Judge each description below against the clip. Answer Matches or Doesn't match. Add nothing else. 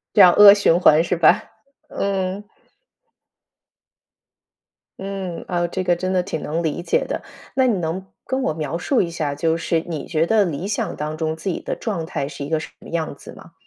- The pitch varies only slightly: Doesn't match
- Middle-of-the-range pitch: Matches